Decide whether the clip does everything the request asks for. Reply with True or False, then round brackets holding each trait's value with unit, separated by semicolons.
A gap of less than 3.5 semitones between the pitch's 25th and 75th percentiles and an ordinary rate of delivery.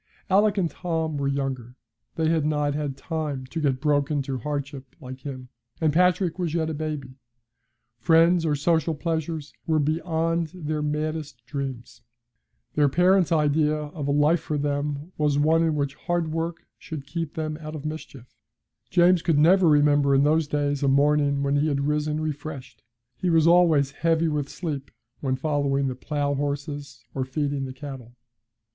True (2.4 semitones; 170 wpm)